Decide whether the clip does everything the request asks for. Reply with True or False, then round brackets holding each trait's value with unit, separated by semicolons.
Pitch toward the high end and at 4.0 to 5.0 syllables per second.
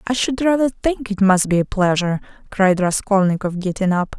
False (200 Hz; 5.4 syllables/s)